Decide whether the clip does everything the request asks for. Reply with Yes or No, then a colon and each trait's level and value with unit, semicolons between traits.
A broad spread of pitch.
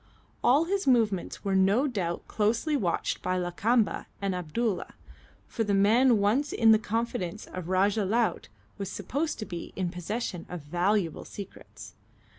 No: average, 4.3 semitones